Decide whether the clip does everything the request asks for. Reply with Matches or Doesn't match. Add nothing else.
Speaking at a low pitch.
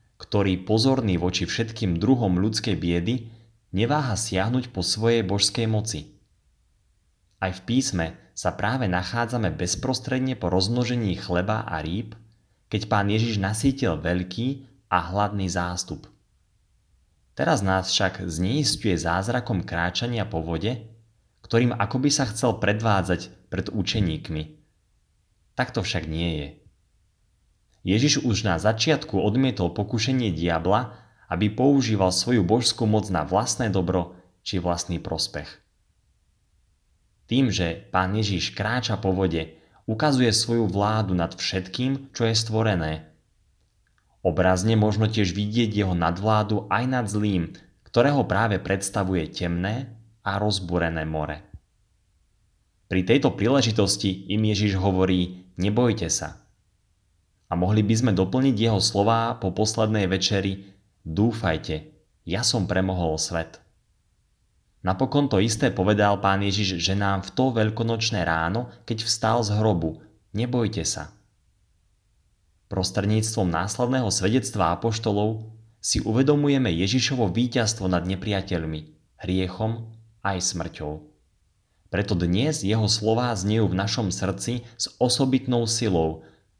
Matches